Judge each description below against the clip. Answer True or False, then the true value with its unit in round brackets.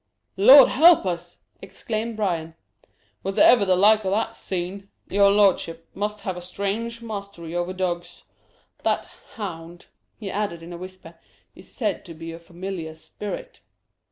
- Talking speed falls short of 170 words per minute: True (150 wpm)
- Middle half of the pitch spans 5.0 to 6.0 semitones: False (3.3 semitones)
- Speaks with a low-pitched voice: False (190 Hz)